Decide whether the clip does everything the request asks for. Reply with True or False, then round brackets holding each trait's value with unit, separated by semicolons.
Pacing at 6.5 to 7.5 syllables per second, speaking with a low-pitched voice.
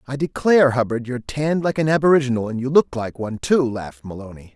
True (6.6 syllables/s; 130 Hz)